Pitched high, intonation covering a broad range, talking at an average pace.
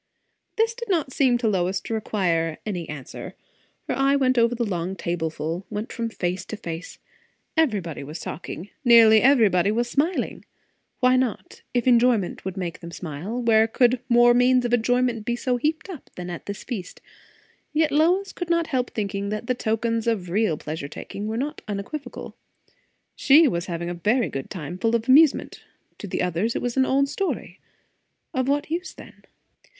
Yes: high, 230 Hz; wide, 5.9 semitones; average, 175 wpm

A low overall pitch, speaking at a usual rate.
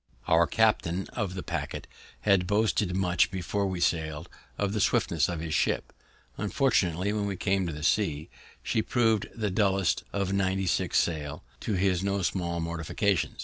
Yes: very low, 95 Hz; average, 160 wpm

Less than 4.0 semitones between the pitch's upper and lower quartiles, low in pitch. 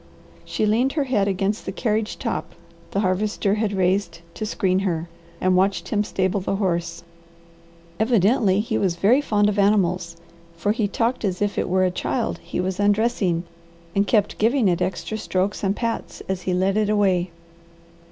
No: narrow, 2.6 semitones; high, 200 Hz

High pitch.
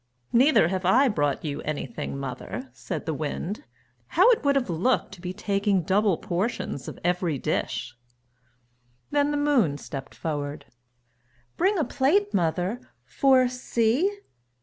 Yes: high, 195 Hz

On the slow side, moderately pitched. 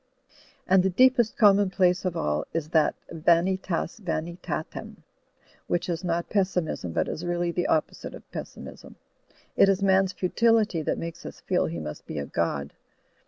No: average, 155 wpm; medium, 175 Hz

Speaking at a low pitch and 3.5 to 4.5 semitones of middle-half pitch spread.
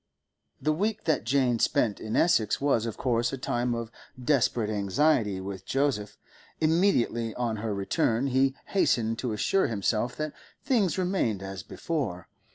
No: low, 120 Hz; average, 5.3 semitones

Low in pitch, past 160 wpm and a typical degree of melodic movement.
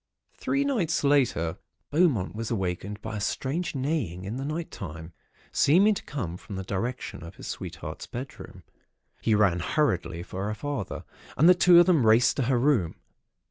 No: low, 120 Hz; average, 175 wpm; wide, 8.0 semitones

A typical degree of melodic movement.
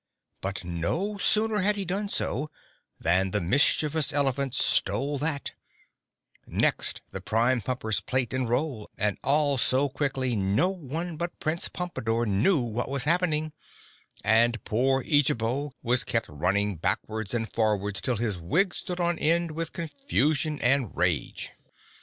No: wide, 6.2 semitones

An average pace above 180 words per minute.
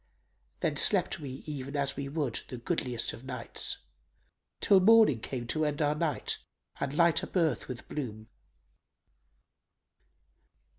No: average, 140 wpm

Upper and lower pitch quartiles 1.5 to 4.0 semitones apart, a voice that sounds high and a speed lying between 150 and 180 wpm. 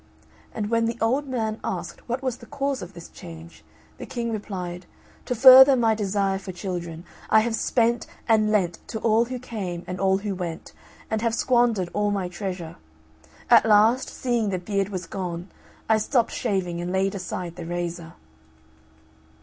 No: average, 4.4 semitones; high, 205 Hz; average, 175 wpm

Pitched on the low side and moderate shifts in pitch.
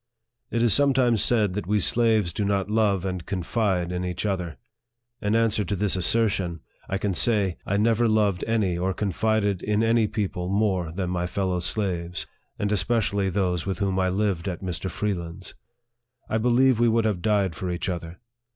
Yes: low, 100 Hz; average, 3.2 semitones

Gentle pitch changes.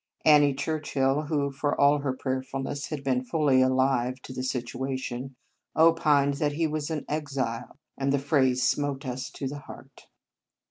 Yes: narrow, 2.0 semitones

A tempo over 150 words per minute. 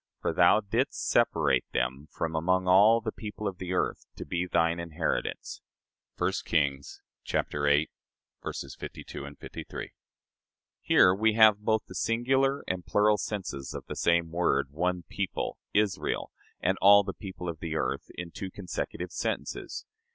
No: average, 145 wpm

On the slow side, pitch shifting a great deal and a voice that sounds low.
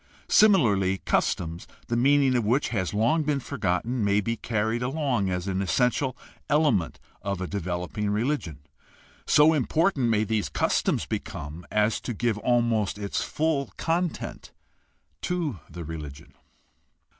Yes: slow, 130 wpm; wide, 6.1 semitones; low, 115 Hz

